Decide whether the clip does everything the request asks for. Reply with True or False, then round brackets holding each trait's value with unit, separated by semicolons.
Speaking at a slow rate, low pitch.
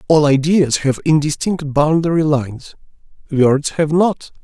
False (120 wpm; 150 Hz)